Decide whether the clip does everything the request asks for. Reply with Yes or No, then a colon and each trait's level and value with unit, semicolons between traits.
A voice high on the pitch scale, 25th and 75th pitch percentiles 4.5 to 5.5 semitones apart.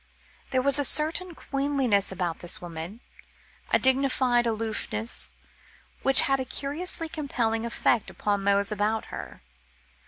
Yes: high, 240 Hz; average, 5.0 semitones